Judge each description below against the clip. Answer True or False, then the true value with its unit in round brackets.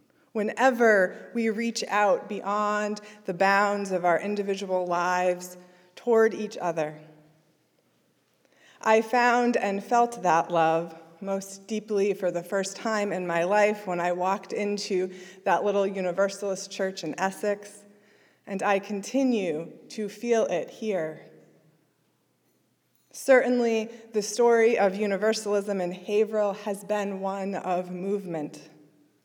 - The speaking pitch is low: False (200 Hz)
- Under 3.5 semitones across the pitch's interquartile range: True (2.8 semitones)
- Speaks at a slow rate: True (120 wpm)